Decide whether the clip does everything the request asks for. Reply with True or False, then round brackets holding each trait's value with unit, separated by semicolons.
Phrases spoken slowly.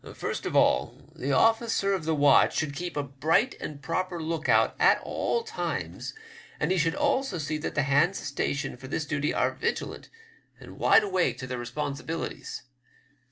False (175 wpm)